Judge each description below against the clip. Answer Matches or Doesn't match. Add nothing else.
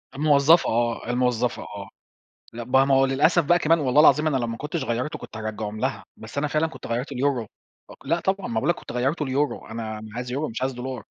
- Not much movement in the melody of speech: Doesn't match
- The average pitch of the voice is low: Matches